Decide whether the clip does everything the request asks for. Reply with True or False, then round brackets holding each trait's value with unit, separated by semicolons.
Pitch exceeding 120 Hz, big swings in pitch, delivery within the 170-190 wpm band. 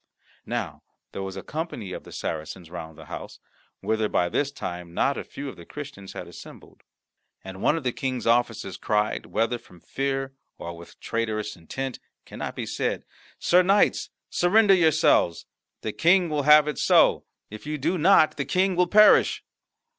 True (135 Hz; 8.4 semitones; 175 wpm)